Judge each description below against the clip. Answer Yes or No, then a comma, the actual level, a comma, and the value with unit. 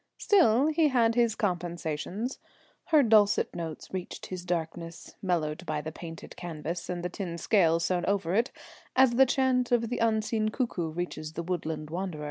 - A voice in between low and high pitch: Yes, medium, 180 Hz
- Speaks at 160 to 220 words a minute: Yes, average, 165 wpm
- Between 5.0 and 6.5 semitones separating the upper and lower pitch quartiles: Yes, wide, 5.6 semitones